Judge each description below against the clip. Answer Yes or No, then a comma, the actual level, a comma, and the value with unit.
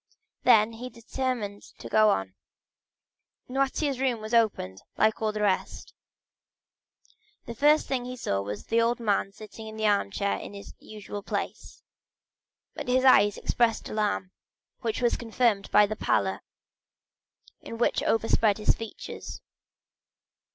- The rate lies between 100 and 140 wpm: Yes, slow, 135 wpm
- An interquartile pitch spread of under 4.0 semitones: Yes, average, 2.7 semitones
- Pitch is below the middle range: No, high, 220 Hz